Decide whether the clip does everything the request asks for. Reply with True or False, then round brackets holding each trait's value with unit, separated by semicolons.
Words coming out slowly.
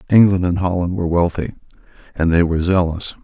False (165 wpm)